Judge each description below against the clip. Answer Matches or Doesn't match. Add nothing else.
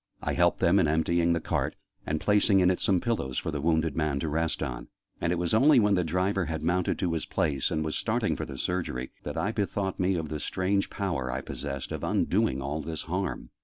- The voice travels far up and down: Doesn't match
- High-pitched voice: Doesn't match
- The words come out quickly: Matches